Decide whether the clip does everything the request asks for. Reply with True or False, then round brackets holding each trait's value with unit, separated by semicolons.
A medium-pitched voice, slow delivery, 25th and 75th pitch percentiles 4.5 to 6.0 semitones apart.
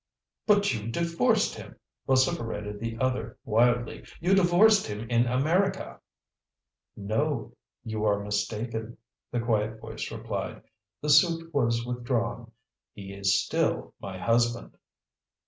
False (115 Hz; 115 wpm; 5.2 semitones)